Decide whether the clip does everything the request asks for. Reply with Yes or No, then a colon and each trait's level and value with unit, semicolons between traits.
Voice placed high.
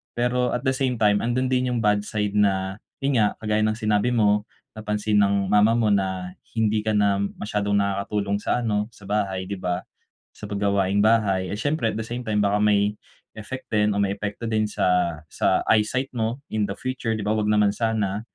No: low, 105 Hz